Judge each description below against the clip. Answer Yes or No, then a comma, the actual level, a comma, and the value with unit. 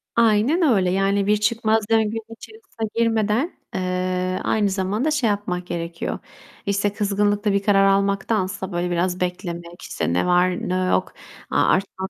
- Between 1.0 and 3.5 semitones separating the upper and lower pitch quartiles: Yes, average, 3.1 semitones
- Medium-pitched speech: No, high, 200 Hz